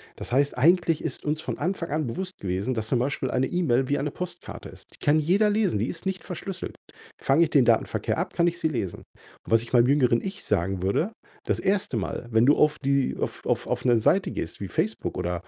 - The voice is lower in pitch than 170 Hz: Yes, medium, 140 Hz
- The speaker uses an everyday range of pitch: No, wide, 6.6 semitones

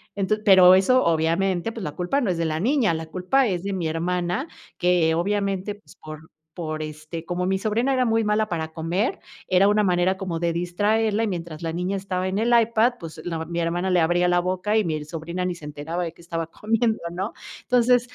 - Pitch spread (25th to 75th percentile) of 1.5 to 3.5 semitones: No, average, 3.9 semitones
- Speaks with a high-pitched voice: No, medium, 180 Hz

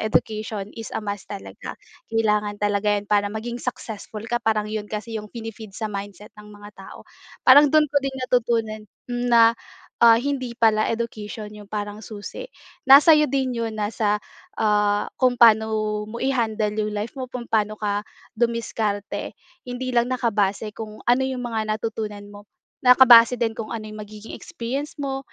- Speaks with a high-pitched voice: Yes, high, 220 Hz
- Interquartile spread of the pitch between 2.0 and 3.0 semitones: Yes, narrow, 2.5 semitones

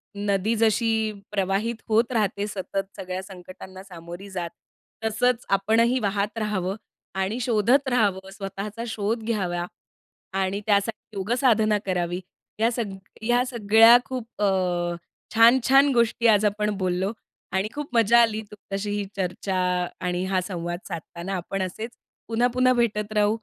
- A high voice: Yes, high, 210 Hz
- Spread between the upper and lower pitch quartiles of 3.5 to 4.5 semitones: No, average, 3.1 semitones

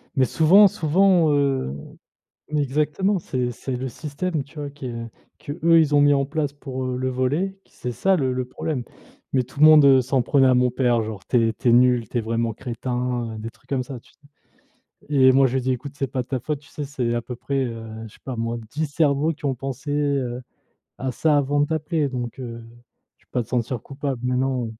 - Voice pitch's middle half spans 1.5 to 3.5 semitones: Yes, average, 2.9 semitones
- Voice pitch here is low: Yes, low, 130 Hz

